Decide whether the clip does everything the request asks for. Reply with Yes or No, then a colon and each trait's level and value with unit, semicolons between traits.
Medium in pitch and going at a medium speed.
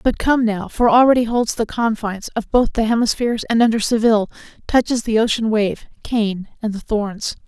No: high, 225 Hz; average, 185 wpm